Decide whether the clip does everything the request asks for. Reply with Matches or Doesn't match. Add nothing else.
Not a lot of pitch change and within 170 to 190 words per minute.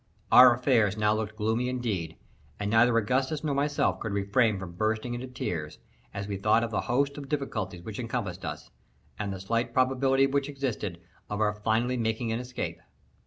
Doesn't match